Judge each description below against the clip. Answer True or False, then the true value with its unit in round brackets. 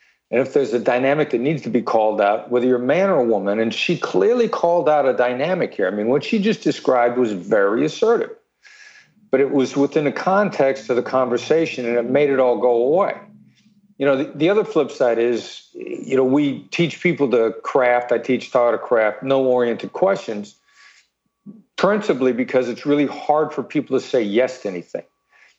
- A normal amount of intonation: False (8.2 semitones)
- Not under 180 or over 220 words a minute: True (200 wpm)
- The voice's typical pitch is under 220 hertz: True (140 Hz)